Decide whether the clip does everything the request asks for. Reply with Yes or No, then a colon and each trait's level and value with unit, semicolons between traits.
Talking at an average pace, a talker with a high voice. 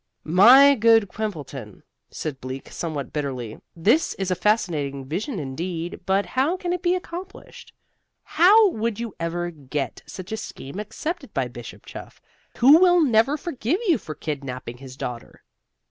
Yes: average, 150 wpm; high, 195 Hz